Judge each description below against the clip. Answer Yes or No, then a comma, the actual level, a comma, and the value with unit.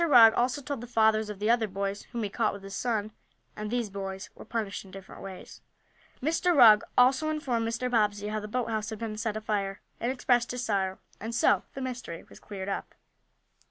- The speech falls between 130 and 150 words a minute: No, fast, 205 wpm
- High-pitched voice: Yes, high, 220 Hz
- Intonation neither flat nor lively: Yes, average, 3.1 semitones